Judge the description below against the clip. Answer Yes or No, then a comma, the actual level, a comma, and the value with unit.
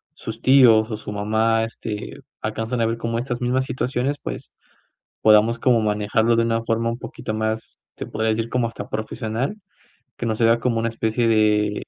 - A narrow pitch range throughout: Yes, narrow, 1.3 semitones